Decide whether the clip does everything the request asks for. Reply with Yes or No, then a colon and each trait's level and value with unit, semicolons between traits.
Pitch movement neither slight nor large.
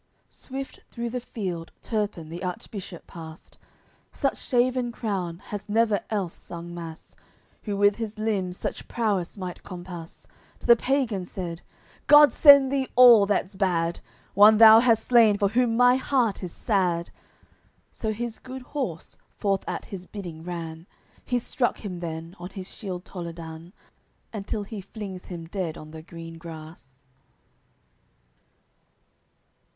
Yes: average, 4.9 semitones